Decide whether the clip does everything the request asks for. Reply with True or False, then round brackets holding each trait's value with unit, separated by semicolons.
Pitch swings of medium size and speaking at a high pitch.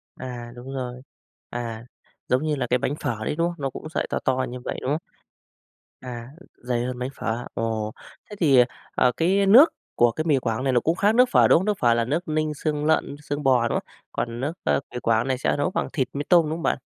False (4.3 semitones; 130 Hz)